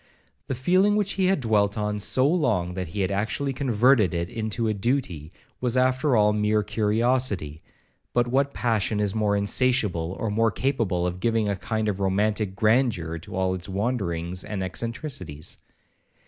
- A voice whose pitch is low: Yes, low, 105 Hz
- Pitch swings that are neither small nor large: Yes, average, 4.7 semitones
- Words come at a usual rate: Yes, average, 165 wpm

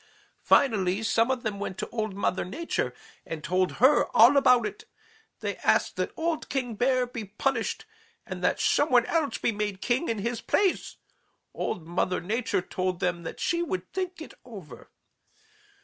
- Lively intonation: Yes, wide, 6.2 semitones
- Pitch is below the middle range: No, high, 230 Hz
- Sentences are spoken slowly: No, average, 170 wpm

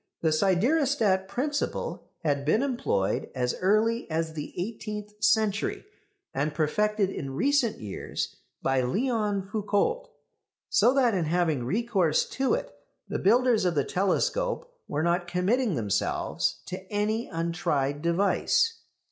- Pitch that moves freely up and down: Yes, wide, 6.6 semitones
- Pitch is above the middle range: Yes, high, 195 Hz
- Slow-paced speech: Yes, slow, 125 wpm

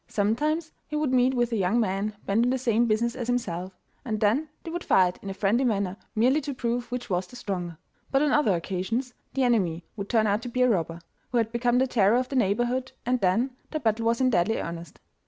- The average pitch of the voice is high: Yes, high, 230 Hz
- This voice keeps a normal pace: No, fast, 235 wpm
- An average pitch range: Yes, average, 4.2 semitones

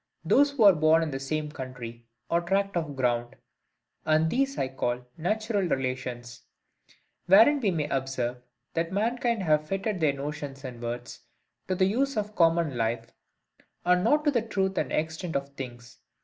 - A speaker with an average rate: Yes, average, 165 wpm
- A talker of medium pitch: Yes, medium, 155 Hz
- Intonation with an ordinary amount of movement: No, wide, 7.1 semitones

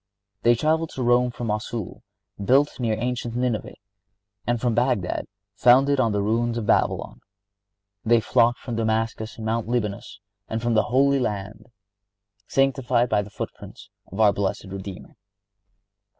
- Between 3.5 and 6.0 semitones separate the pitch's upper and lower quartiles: No, narrow, 2.5 semitones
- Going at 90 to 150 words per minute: Yes, average, 145 wpm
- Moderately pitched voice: No, low, 115 Hz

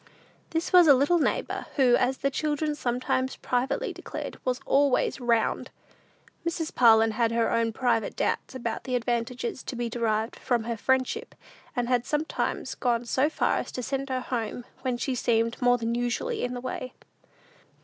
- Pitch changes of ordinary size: No, narrow, 2.2 semitones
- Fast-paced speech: No, average, 170 wpm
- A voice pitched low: No, high, 245 Hz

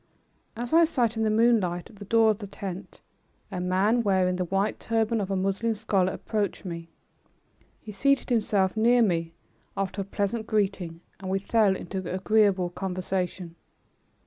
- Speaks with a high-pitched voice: Yes, high, 200 Hz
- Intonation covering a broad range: No, average, 3.0 semitones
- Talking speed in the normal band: Yes, average, 165 wpm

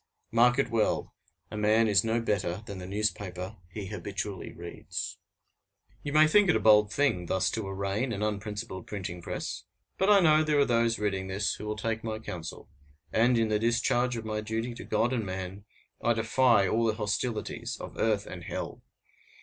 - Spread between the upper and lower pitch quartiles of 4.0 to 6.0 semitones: No, average, 2.9 semitones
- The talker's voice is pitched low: Yes, low, 110 Hz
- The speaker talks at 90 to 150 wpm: No, average, 190 wpm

